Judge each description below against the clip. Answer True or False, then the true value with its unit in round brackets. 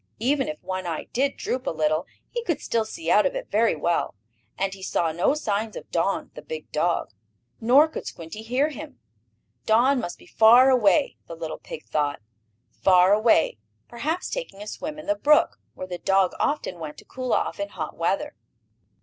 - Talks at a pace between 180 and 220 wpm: True (190 wpm)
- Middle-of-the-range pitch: False (220 Hz)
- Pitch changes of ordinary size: False (8.1 semitones)